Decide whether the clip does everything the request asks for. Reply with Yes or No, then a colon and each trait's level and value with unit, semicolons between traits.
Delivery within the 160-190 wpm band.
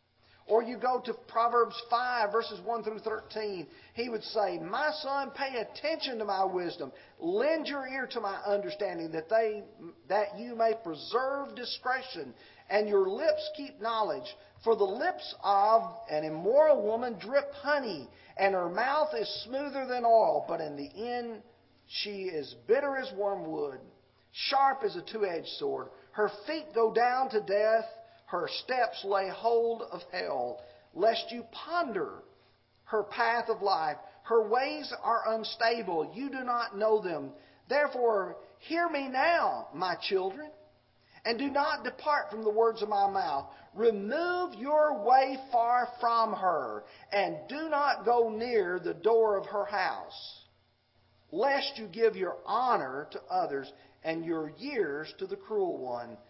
No: average, 150 wpm